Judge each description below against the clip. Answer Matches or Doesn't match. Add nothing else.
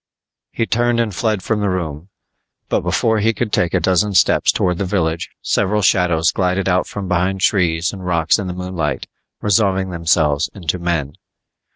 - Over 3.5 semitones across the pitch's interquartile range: Doesn't match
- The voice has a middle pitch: Doesn't match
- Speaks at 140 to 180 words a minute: Matches